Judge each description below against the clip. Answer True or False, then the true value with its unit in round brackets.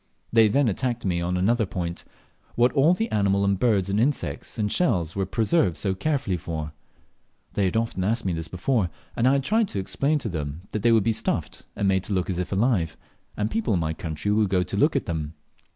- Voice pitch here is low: True (100 Hz)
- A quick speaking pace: True (230 wpm)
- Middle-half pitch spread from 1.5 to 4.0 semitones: False (4.7 semitones)